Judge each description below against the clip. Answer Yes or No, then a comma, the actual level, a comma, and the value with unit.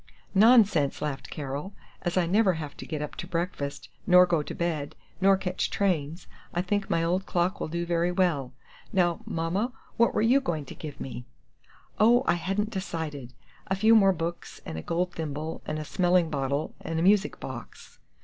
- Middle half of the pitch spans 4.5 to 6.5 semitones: No, average, 3.8 semitones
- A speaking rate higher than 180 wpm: Yes, average, 190 wpm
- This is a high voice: No, medium, 175 Hz